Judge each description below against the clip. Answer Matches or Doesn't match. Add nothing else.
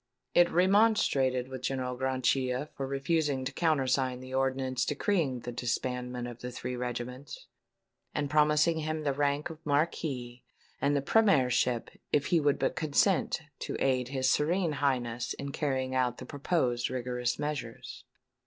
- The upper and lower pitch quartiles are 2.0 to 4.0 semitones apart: Matches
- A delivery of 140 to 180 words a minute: Matches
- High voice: Doesn't match